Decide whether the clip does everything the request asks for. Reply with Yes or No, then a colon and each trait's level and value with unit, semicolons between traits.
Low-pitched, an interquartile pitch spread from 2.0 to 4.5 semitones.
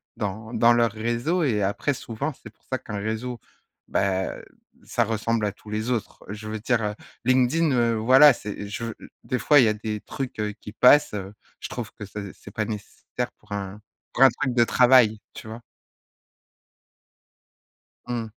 Yes: low, 110 Hz; average, 2.9 semitones